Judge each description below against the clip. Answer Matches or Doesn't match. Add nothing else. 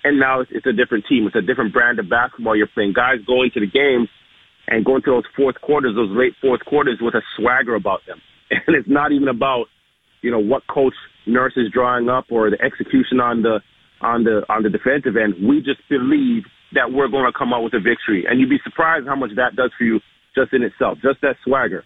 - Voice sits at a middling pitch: Doesn't match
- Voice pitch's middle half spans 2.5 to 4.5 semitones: Matches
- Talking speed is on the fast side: Matches